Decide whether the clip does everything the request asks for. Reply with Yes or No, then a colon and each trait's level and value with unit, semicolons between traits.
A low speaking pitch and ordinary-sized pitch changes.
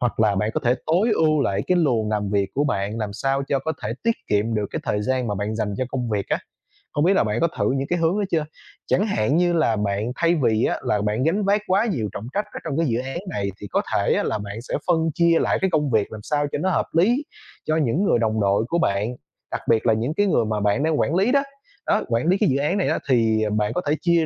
No: low, 130 Hz; wide, 7.6 semitones